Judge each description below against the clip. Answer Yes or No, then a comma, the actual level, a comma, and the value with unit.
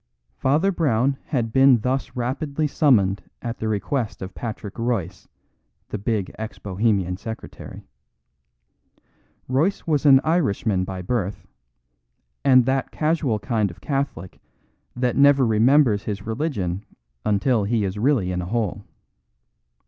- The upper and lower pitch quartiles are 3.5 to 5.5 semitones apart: Yes, average, 5.2 semitones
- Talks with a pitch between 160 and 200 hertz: No, low, 115 Hz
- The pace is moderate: No, slow, 125 wpm